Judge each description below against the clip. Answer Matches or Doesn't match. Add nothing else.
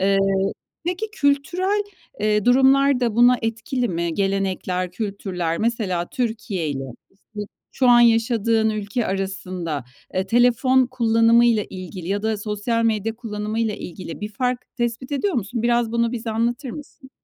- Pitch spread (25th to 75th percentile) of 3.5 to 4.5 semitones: Matches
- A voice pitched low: Doesn't match